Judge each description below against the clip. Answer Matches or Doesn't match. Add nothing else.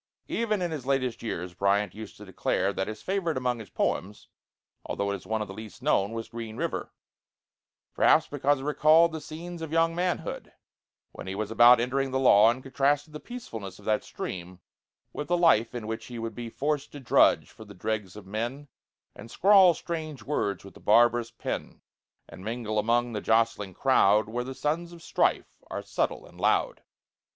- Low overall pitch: Matches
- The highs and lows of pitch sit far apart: Matches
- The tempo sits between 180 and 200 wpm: Matches